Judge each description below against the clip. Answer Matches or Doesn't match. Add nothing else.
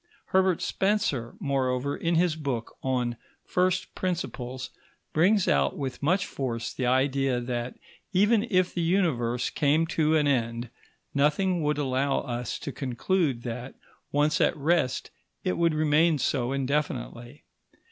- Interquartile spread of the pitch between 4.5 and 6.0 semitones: Matches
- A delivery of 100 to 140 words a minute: Matches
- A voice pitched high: Doesn't match